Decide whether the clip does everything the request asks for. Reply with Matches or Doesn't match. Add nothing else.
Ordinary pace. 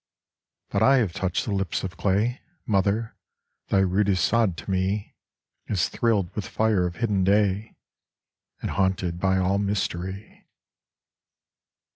Doesn't match